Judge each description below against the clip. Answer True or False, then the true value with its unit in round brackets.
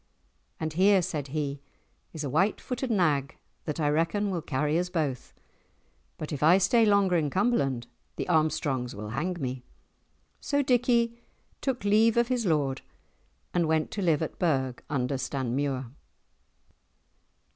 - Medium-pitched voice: True (160 Hz)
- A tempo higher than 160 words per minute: False (145 wpm)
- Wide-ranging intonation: True (6.5 semitones)